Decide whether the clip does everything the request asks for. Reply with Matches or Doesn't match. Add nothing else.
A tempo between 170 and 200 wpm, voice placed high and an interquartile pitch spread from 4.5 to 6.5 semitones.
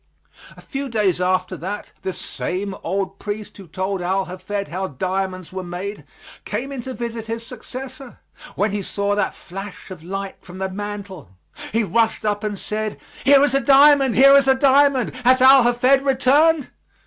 Matches